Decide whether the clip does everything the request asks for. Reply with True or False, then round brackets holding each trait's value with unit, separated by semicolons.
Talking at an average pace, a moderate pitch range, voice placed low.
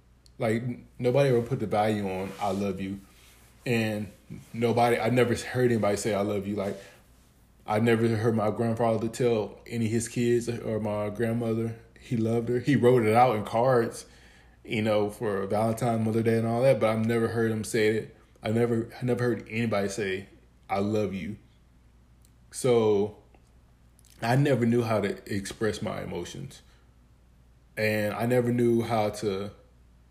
True (165 wpm; 3.0 semitones; 110 Hz)